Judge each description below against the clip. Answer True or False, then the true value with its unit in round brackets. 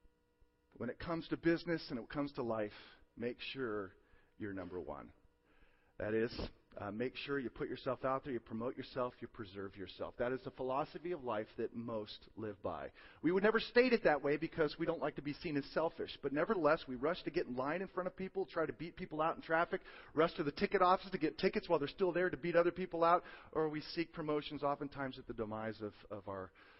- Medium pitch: True (145 Hz)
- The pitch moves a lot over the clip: True (6.1 semitones)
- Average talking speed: False (235 wpm)